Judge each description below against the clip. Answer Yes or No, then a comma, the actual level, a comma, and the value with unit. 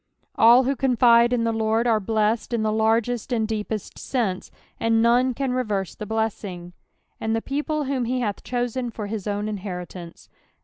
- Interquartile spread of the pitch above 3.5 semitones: No, narrow, 2.5 semitones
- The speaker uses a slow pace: No, average, 175 wpm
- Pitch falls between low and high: No, high, 225 Hz